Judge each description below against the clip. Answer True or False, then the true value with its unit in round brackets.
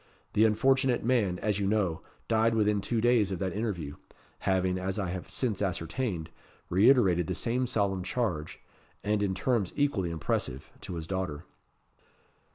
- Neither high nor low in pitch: False (100 Hz)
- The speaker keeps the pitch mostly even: False (4.0 semitones)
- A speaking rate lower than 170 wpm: True (155 wpm)